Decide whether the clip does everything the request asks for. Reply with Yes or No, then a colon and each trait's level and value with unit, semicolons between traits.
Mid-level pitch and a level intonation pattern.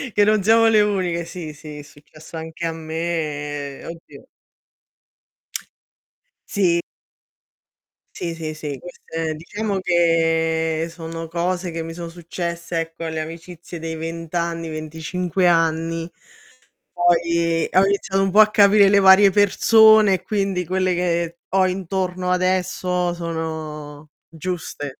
Yes: medium, 170 Hz; narrow, 2.3 semitones